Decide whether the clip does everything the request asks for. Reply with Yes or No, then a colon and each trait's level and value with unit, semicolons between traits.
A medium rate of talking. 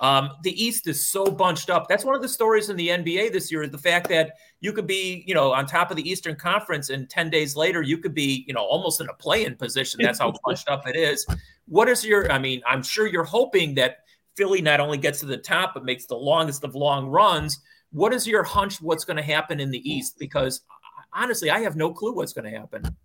No: fast, 255 wpm